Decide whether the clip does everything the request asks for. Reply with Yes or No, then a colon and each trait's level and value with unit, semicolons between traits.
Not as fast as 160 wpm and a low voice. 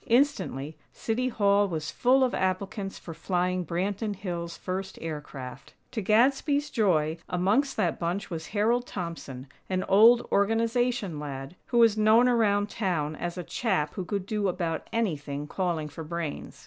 No: average, 150 wpm; high, 190 Hz